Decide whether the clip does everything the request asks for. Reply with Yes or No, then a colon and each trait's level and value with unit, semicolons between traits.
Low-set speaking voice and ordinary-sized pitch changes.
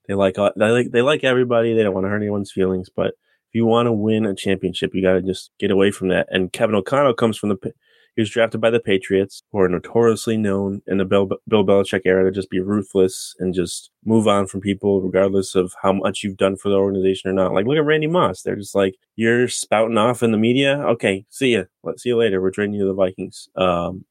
Yes: low, 100 Hz; average, 3.2 semitones